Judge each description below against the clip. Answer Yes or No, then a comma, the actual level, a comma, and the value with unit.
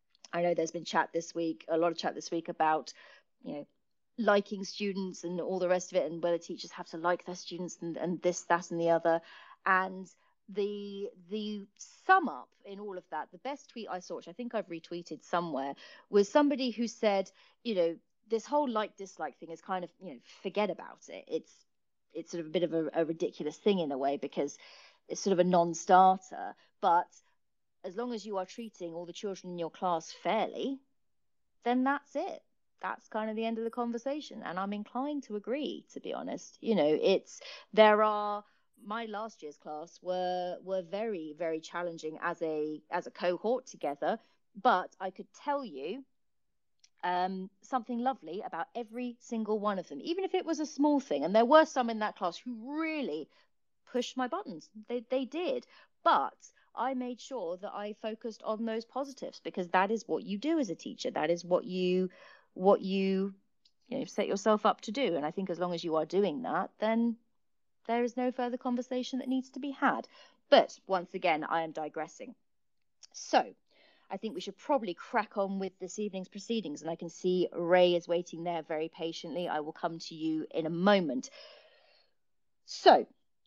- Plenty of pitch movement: Yes, wide, 5.8 semitones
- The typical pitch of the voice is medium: No, high, 200 Hz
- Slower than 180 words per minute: No, average, 200 wpm